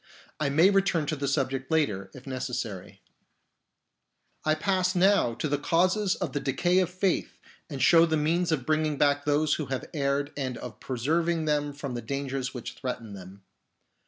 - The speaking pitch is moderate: Yes, medium, 145 Hz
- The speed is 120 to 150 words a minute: No, average, 175 wpm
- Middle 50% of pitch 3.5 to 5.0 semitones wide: Yes, average, 4.0 semitones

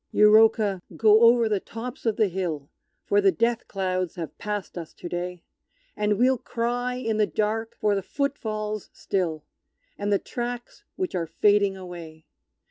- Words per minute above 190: No, average, 165 wpm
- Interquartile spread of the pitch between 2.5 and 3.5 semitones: No, average, 3.9 semitones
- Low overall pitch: No, high, 210 Hz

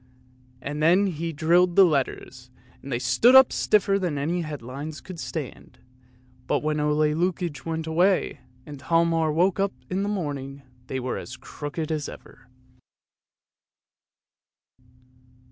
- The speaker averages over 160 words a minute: No, average, 140 wpm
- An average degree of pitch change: Yes, average, 3.8 semitones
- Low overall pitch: No, medium, 155 Hz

